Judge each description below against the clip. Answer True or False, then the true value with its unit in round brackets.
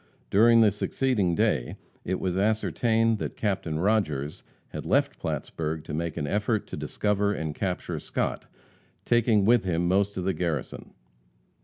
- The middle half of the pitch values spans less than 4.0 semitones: False (4.7 semitones)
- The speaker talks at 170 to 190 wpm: False (150 wpm)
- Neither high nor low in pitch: False (95 Hz)